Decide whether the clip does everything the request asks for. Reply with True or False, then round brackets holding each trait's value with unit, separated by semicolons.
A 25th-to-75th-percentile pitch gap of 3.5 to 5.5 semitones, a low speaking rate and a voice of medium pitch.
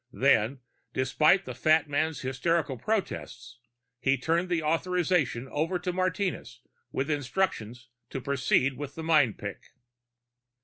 True (4.6 semitones; 125 wpm; 150 Hz)